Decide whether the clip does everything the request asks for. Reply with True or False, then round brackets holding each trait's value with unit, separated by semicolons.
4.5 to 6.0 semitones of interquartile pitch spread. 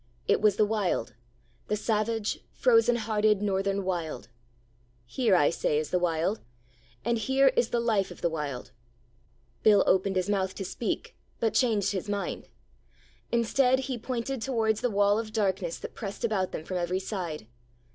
False (3.4 semitones)